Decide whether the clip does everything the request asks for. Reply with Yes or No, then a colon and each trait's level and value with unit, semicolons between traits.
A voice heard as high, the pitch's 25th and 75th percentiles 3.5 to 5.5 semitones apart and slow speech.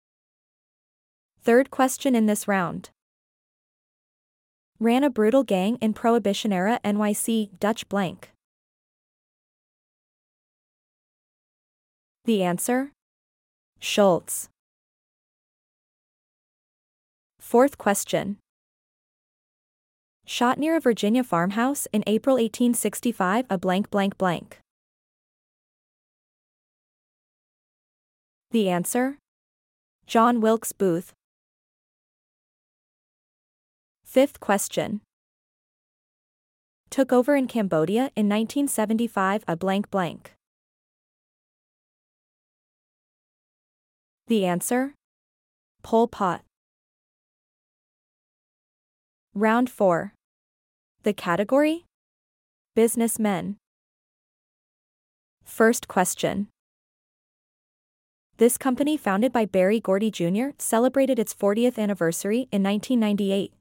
Yes: high, 215 Hz; average, 3.8 semitones; slow, 70 wpm